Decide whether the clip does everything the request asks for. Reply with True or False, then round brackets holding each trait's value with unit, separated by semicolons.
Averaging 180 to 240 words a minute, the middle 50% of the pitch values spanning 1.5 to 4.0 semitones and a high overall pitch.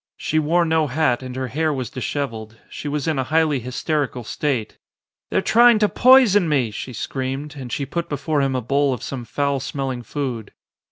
False (200 wpm; 3.6 semitones; 140 Hz)